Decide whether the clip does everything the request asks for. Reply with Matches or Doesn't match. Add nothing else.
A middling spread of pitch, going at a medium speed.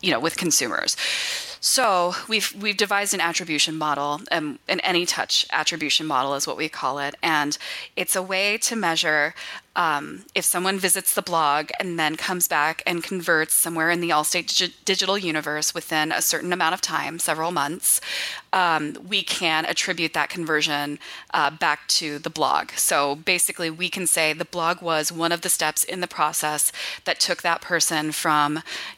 Matches